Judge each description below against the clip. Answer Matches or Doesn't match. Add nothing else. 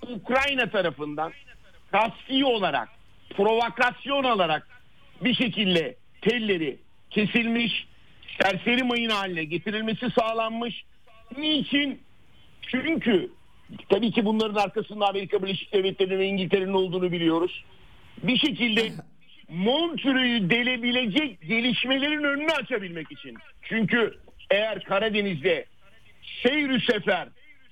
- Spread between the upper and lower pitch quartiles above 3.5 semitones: Matches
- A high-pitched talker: Matches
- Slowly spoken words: Matches